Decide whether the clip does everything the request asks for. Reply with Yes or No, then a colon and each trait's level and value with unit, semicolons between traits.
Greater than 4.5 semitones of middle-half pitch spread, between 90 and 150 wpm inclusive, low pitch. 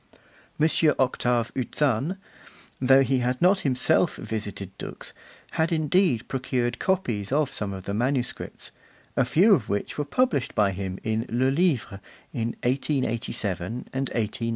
Yes: average, 5.0 semitones; average, 140 wpm; low, 125 Hz